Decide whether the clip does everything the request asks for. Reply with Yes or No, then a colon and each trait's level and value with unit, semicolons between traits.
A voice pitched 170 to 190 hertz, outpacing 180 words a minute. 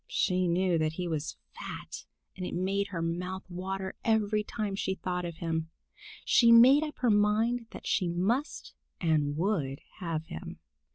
No: medium, 185 Hz; average, 165 wpm